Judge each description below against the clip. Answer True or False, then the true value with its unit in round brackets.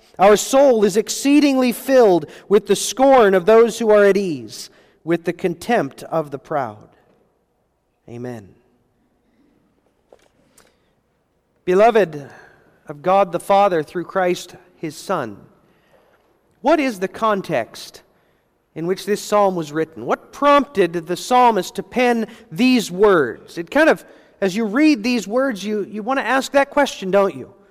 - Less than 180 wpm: True (140 wpm)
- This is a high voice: True (200 Hz)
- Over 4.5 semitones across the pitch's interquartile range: True (5.4 semitones)